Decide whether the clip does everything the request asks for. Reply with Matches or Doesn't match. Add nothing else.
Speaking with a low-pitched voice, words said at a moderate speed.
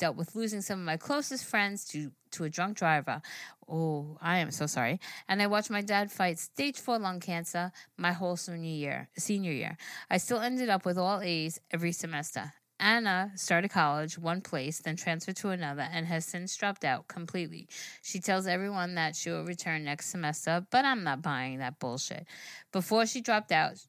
Doesn't match